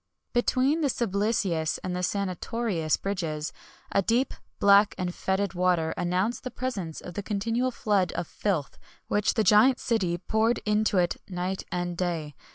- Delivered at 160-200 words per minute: No, average, 150 wpm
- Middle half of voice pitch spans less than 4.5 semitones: Yes, average, 4.0 semitones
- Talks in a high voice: Yes, high, 195 Hz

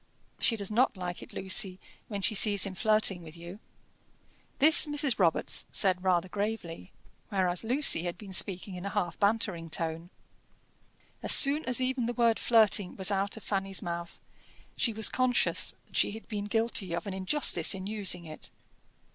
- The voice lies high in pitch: Yes, high, 200 Hz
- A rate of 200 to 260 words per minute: No, average, 170 wpm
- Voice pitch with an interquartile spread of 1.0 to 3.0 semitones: No, average, 3.8 semitones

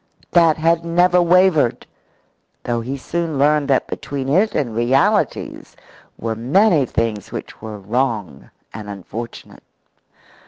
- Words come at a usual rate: No, slow, 120 wpm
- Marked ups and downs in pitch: Yes, wide, 6.5 semitones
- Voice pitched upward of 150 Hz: No, low, 135 Hz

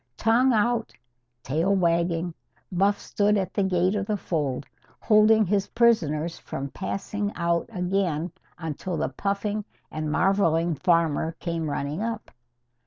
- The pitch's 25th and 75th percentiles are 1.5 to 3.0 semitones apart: No, average, 4.0 semitones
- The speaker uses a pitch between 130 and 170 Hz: No, medium, 180 Hz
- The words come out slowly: Yes, slow, 130 wpm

